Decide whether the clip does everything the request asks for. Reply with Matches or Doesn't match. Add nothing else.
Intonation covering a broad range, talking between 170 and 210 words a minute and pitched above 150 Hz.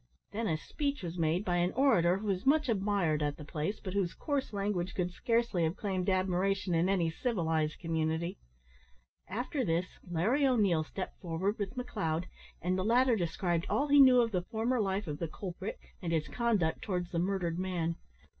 Doesn't match